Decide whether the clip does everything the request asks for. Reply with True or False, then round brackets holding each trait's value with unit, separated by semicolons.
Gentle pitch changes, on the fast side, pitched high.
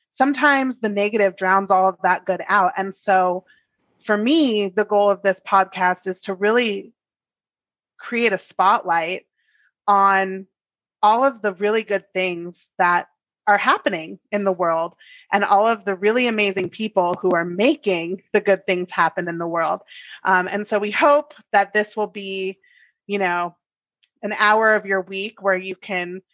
False (2.3 semitones; 165 wpm; 195 Hz)